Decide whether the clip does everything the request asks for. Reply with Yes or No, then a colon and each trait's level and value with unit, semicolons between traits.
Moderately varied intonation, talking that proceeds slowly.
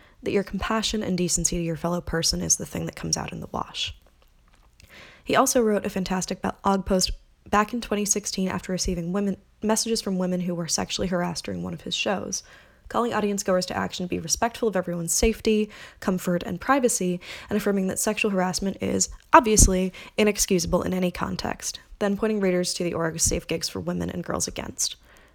No: average, 3.2 semitones; average, 190 wpm